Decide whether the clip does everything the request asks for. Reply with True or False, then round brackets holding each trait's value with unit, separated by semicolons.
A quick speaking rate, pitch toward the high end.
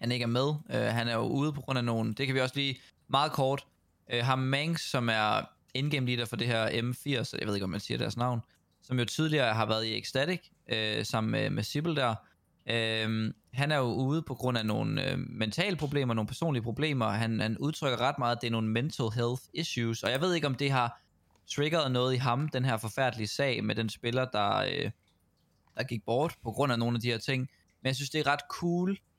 False (240 wpm; 125 Hz)